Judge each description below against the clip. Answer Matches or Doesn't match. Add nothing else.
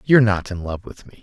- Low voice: Matches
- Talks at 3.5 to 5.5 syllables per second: Doesn't match